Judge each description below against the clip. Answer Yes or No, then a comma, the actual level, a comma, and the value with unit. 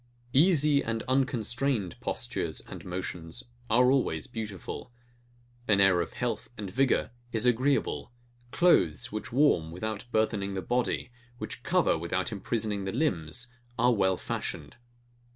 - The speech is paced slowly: Yes, slow, 130 wpm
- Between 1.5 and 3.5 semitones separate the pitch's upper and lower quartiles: No, average, 4.8 semitones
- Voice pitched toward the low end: Yes, low, 110 Hz